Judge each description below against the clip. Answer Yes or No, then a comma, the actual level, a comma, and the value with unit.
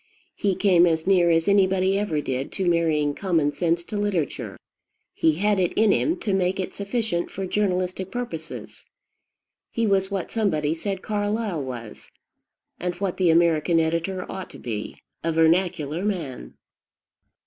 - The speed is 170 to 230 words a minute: No, average, 150 wpm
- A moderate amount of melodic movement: Yes, average, 3.4 semitones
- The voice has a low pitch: No, medium, 180 Hz